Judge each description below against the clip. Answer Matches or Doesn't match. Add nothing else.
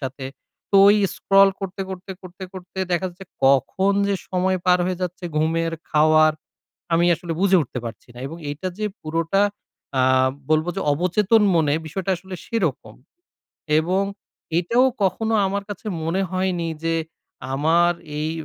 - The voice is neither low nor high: Matches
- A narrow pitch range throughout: Doesn't match